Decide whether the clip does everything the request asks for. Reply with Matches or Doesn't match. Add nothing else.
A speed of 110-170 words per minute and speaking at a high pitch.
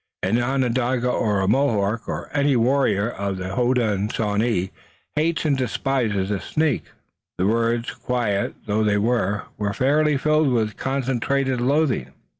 Doesn't match